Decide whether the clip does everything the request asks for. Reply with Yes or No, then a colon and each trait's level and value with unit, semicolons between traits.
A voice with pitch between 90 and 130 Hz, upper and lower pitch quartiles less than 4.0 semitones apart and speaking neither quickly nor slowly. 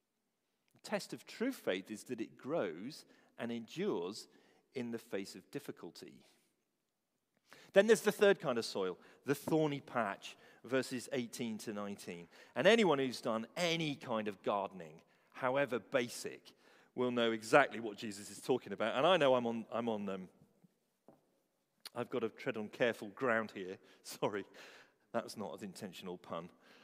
No: low, 115 Hz; average, 4.3 semitones; average, 155 wpm